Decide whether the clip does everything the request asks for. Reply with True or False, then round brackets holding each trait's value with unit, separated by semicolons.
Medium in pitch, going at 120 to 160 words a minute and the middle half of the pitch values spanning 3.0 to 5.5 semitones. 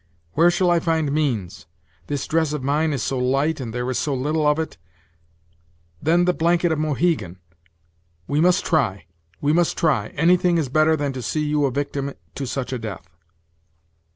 False (150 Hz; 180 wpm; 3.5 semitones)